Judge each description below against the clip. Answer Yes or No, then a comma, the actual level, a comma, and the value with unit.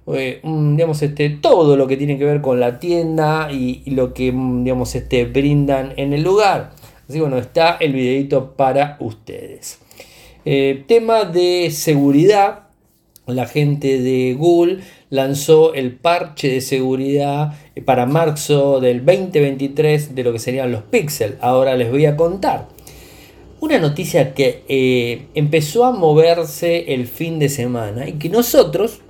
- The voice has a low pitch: No, medium, 145 Hz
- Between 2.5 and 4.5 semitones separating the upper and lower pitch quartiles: Yes, average, 3.8 semitones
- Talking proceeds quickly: No, average, 145 wpm